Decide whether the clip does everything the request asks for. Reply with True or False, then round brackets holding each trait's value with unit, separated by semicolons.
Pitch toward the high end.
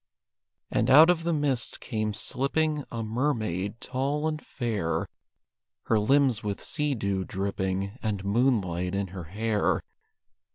False (110 Hz)